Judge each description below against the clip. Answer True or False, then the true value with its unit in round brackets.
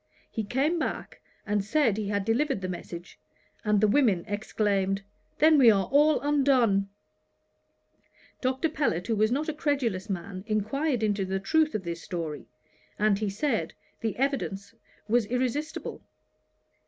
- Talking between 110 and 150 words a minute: True (145 wpm)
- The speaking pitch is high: True (215 Hz)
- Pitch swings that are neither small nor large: False (5.9 semitones)